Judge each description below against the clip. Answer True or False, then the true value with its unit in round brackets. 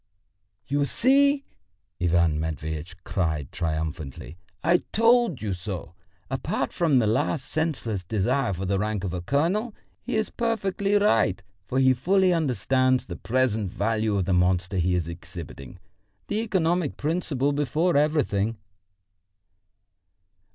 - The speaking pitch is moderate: False (120 Hz)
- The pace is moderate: False (130 wpm)